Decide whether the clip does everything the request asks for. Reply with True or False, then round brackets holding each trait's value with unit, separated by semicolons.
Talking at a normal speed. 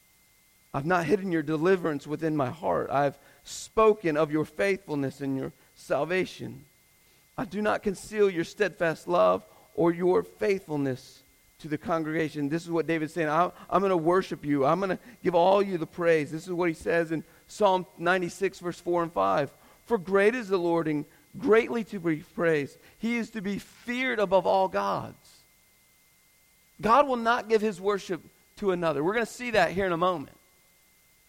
True (180 wpm)